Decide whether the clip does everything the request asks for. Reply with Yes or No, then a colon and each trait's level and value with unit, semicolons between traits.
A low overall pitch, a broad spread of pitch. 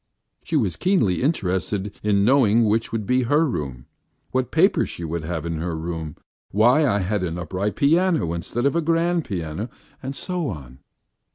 Yes: low, 105 Hz; wide, 8.6 semitones